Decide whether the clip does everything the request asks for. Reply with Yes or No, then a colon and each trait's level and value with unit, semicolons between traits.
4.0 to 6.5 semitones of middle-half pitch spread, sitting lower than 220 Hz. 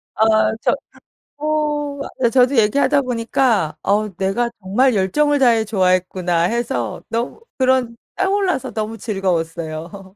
No: wide, 5.6 semitones; high, 230 Hz